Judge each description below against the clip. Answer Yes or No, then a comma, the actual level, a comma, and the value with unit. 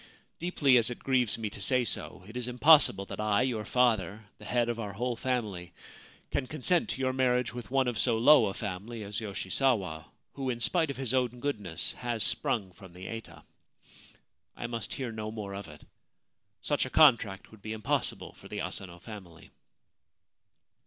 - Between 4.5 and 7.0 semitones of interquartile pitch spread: No, average, 3.8 semitones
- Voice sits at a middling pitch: No, low, 115 Hz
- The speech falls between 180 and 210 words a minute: Yes, average, 185 wpm